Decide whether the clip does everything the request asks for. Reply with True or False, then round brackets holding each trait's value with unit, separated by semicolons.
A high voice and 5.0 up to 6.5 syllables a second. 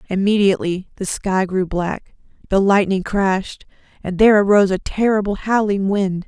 True (195 Hz; 5.1 syllables/s)